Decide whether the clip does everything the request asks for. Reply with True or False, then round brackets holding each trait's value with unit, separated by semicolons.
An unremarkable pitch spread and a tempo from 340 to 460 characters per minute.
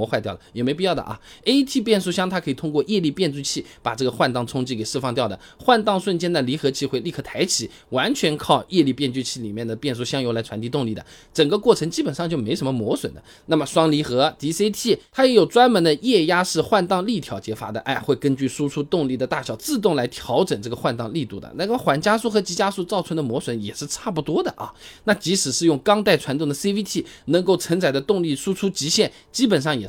False (6.6 semitones; 365 characters per minute)